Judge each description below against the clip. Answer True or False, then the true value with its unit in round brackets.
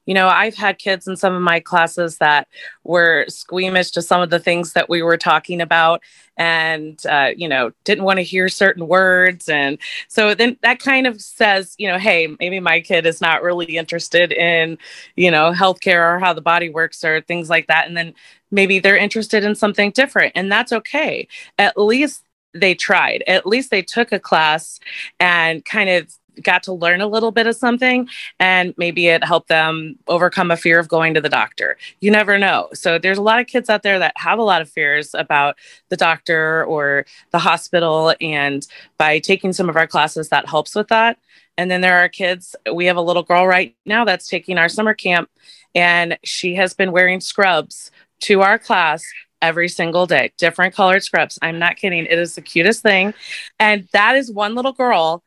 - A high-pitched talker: False (180 Hz)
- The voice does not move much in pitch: False (3.2 semitones)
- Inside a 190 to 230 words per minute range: True (205 wpm)